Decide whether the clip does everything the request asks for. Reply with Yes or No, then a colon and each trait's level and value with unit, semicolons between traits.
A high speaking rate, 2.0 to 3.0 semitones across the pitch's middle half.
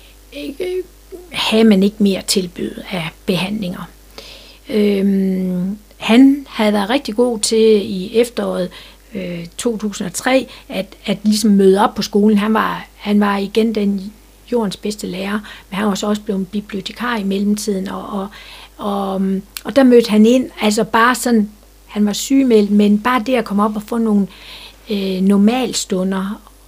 No: average, 155 wpm; narrow, 2.5 semitones